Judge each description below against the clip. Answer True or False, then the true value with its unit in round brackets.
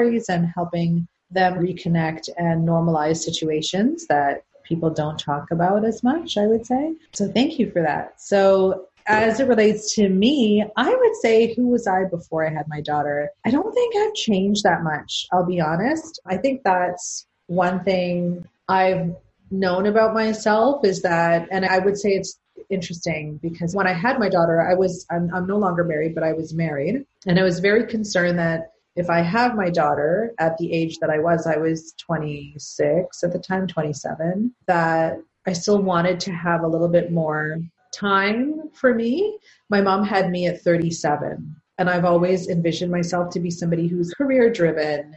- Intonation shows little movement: False (4.0 semitones)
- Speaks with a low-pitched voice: False (180 Hz)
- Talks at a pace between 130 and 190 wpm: True (180 wpm)